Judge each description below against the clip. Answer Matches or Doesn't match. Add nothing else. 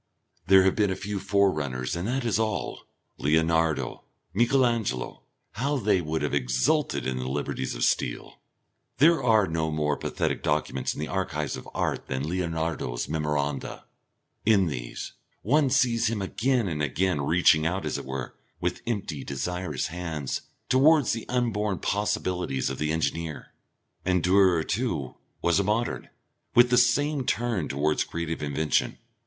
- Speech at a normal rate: Matches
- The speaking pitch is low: Matches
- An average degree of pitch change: Doesn't match